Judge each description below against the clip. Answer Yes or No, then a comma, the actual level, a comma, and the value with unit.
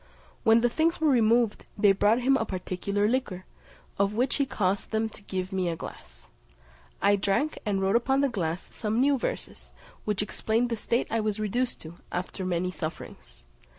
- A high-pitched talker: Yes, high, 210 Hz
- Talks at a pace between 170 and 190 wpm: Yes, average, 185 wpm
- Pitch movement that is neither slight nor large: Yes, average, 4.1 semitones